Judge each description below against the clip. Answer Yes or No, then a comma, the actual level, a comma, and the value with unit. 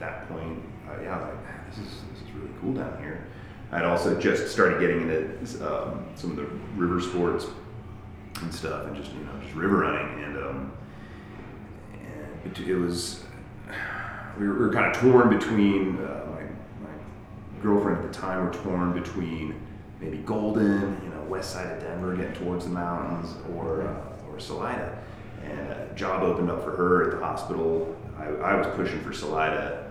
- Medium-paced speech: Yes, average, 185 wpm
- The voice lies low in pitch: Yes, very low, 95 Hz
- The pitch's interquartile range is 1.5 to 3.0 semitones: No, average, 3.6 semitones